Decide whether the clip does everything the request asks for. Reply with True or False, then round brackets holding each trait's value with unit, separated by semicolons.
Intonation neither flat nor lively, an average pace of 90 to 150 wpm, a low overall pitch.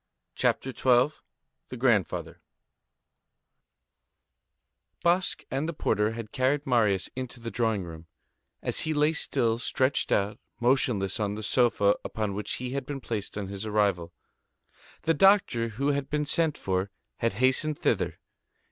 True (5.0 semitones; 140 wpm; 120 Hz)